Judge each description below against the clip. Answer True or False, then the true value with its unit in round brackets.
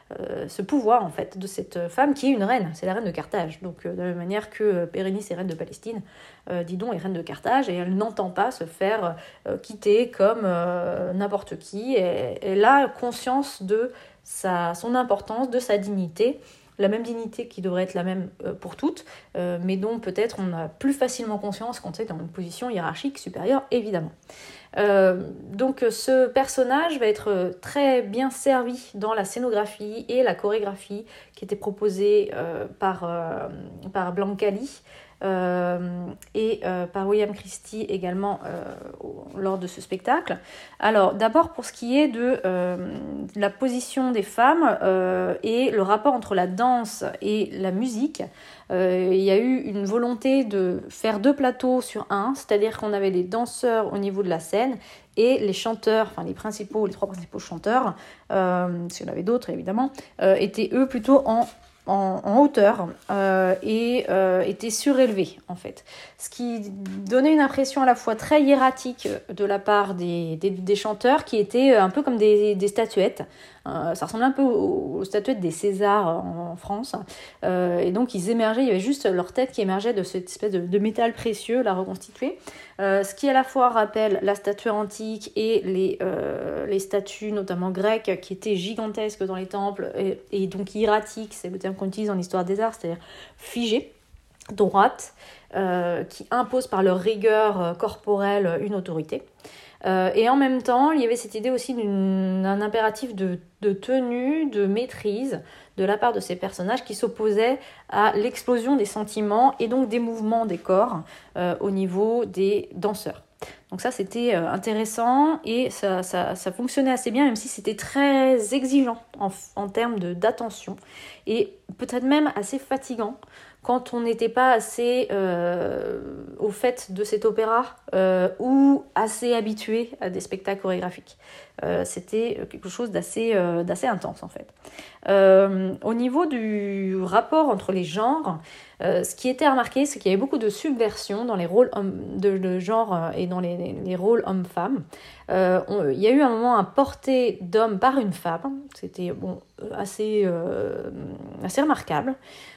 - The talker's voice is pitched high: True (210 Hz)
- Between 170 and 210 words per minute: True (175 wpm)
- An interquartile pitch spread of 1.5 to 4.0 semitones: False (4.4 semitones)